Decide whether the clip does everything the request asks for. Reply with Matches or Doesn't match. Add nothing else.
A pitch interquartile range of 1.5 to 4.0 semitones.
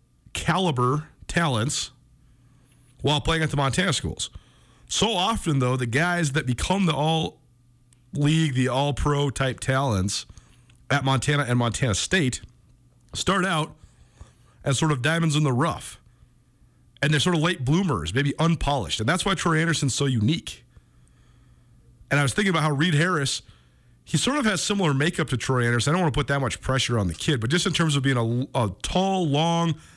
Doesn't match